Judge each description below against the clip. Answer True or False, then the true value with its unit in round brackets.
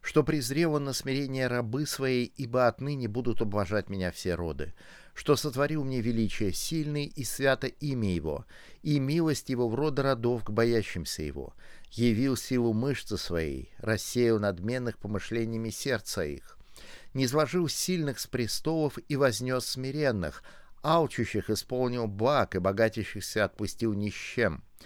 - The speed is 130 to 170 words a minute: True (140 wpm)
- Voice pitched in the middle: False (120 Hz)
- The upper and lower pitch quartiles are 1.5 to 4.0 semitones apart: False (4.7 semitones)